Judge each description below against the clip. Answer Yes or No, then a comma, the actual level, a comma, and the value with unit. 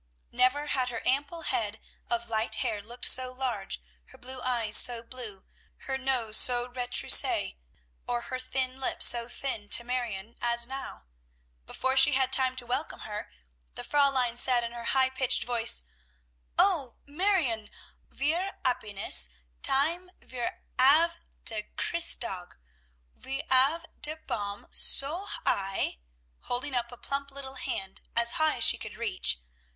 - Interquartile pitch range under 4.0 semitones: Yes, average, 2.7 semitones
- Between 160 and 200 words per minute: No, average, 145 wpm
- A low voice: No, very high, 250 Hz